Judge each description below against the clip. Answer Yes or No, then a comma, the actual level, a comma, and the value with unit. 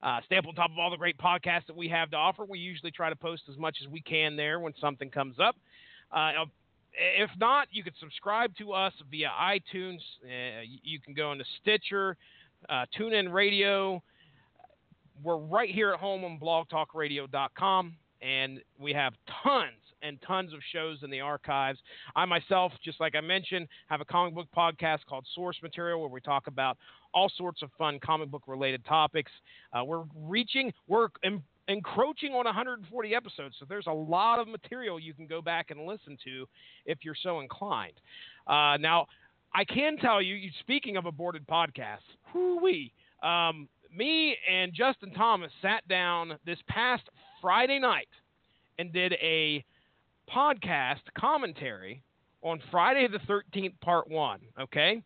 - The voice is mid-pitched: Yes, medium, 170 Hz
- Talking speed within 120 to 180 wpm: Yes, average, 165 wpm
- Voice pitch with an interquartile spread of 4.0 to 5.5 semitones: Yes, average, 4.4 semitones